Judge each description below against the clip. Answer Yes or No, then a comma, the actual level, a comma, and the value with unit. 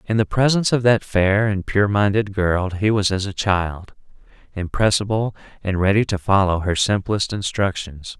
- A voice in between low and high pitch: No, low, 100 Hz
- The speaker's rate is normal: Yes, average, 170 wpm